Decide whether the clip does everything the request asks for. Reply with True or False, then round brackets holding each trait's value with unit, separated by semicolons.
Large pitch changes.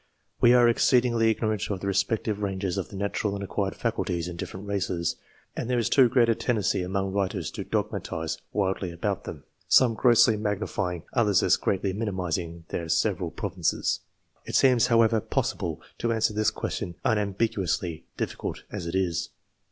False (3.5 semitones)